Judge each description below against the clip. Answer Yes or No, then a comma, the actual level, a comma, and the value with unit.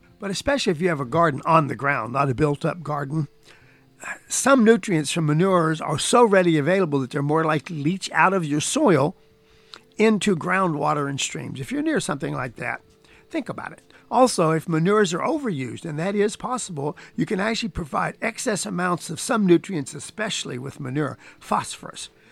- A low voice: No, medium, 170 Hz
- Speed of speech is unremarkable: Yes, average, 185 wpm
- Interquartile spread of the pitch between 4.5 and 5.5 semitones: Yes, average, 5.2 semitones